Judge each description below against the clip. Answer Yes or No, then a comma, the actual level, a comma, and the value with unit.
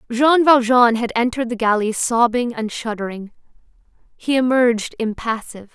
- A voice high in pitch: Yes, high, 235 Hz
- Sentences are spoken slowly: Yes, slow, 125 wpm